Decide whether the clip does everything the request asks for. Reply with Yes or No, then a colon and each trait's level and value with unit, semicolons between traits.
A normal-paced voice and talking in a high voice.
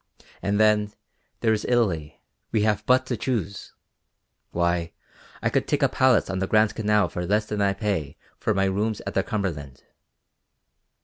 No: average, 170 wpm; low, 105 Hz